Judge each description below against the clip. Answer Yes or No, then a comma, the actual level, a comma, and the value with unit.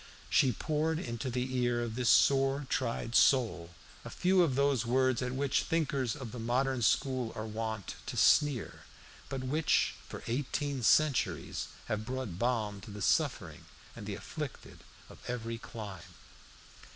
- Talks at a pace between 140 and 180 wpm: Yes, average, 150 wpm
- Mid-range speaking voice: No, low, 125 Hz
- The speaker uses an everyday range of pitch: Yes, average, 3.2 semitones